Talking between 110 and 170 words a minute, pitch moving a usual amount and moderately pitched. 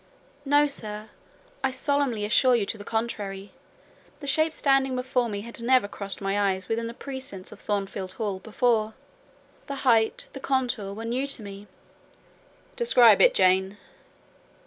No: average, 150 wpm; average, 4.5 semitones; high, 230 Hz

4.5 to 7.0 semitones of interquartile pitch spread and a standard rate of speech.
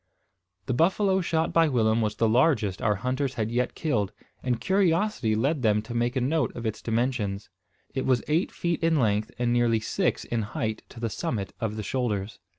Yes: average, 4.8 semitones; average, 195 wpm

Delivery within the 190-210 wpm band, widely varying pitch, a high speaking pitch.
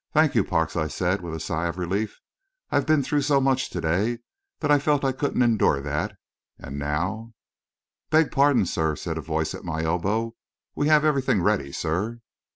No: average, 195 wpm; wide, 9.0 semitones; low, 100 Hz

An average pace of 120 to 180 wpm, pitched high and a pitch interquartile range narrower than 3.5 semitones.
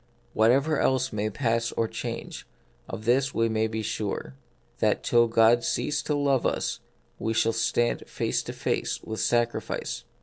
No: average, 160 wpm; low, 115 Hz; narrow, 2.6 semitones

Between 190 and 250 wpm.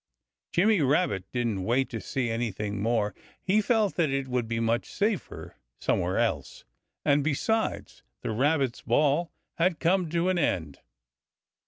No: average, 145 wpm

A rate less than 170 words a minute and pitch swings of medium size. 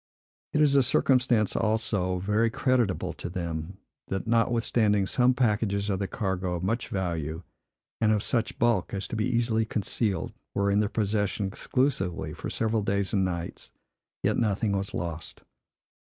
Yes: average, 155 wpm; average, 3.3 semitones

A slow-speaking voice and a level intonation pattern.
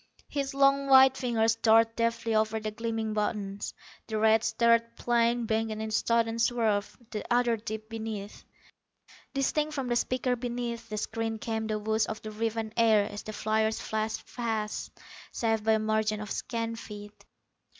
No: average, 165 wpm; narrow, 1.3 semitones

